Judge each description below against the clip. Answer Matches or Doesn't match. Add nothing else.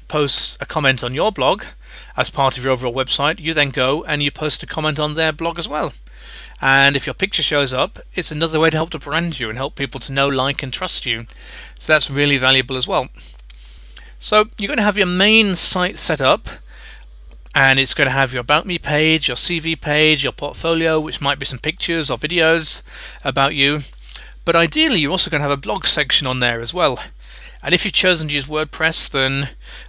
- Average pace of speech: Doesn't match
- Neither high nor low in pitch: Matches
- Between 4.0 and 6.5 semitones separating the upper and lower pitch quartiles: Doesn't match